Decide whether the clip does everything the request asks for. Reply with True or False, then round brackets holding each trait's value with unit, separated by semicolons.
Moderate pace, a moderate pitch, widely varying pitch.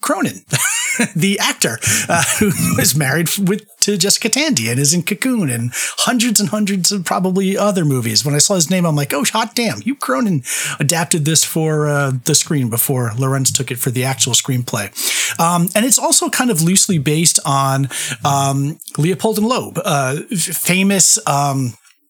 True (180 wpm; 170 Hz; 6.7 semitones)